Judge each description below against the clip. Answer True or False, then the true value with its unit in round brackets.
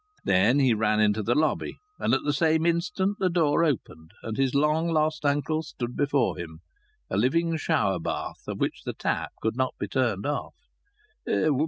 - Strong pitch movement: True (6.1 semitones)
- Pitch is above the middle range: False (140 Hz)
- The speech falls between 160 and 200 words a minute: True (180 wpm)